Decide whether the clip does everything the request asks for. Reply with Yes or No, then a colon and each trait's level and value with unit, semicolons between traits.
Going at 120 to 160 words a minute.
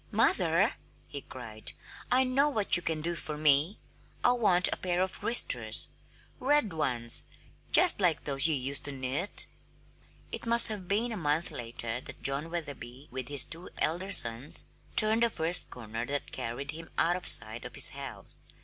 No: average, 175 wpm